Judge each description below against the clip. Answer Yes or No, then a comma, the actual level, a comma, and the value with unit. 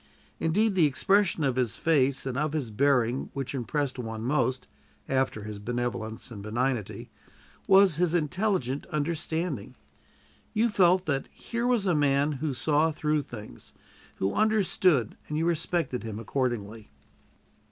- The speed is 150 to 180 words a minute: No, average, 140 wpm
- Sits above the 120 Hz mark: Yes, medium, 140 Hz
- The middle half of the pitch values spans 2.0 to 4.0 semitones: No, wide, 5.6 semitones